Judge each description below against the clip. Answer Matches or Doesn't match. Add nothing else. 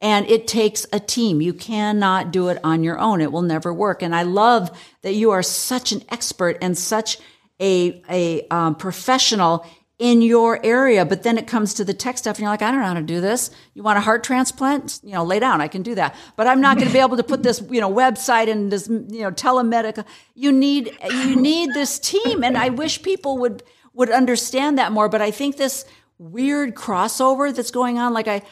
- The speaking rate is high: Matches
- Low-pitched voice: Doesn't match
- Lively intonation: Doesn't match